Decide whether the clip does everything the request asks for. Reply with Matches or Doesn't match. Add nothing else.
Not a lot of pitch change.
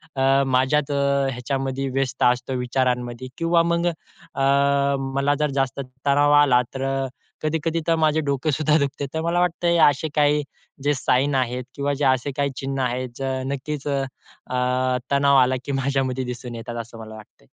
Matches